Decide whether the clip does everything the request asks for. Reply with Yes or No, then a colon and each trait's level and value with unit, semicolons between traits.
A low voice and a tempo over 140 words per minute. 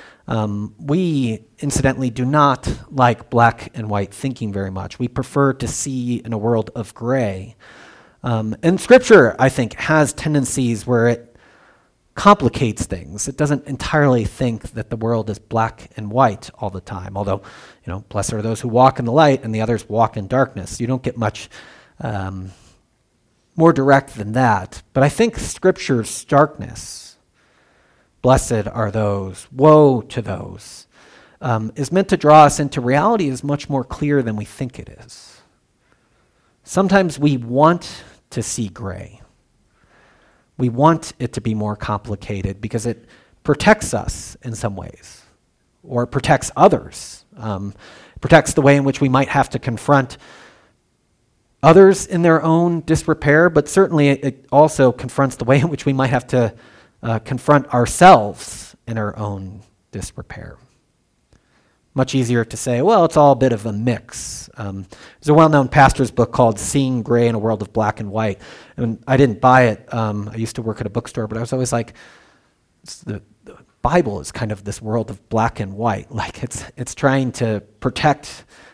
Yes: low, 120 Hz; average, 170 wpm